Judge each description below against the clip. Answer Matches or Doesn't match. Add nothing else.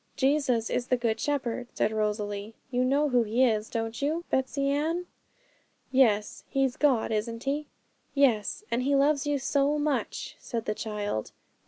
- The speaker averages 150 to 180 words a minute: Matches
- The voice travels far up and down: Doesn't match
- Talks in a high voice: Matches